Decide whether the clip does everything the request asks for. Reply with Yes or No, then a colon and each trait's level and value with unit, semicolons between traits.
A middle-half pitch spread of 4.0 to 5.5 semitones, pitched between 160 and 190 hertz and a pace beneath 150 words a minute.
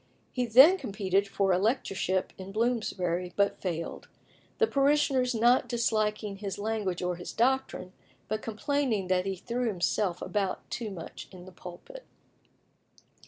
No: average, 4.5 semitones; high, 210 Hz; average, 140 wpm